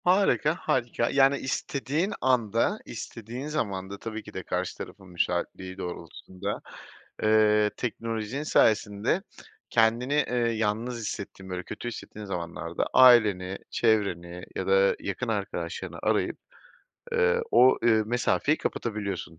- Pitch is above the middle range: No, low, 110 Hz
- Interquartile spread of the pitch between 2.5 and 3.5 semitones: No, average, 4.5 semitones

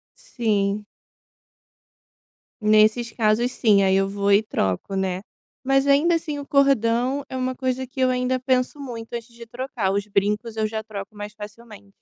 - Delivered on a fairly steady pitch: No, average, 3.8 semitones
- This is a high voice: Yes, high, 230 Hz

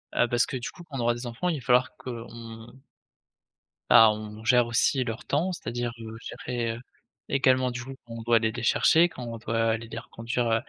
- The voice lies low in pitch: Yes, low, 120 Hz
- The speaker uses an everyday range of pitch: No, narrow, 1.8 semitones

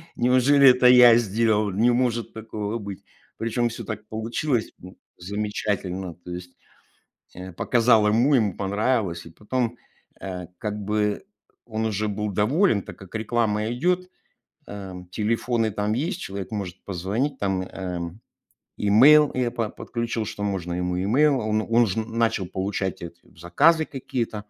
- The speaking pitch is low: Yes, low, 110 Hz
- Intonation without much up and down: No, average, 3.7 semitones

